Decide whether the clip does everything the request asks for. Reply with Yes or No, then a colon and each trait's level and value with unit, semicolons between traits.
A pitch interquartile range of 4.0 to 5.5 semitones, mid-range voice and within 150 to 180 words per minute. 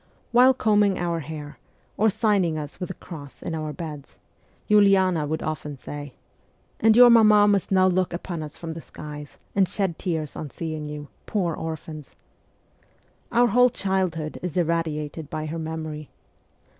Yes: average, 4.3 semitones; medium, 165 Hz; average, 160 wpm